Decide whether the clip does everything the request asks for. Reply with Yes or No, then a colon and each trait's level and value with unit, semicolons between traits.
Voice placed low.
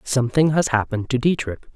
Yes: low, 130 Hz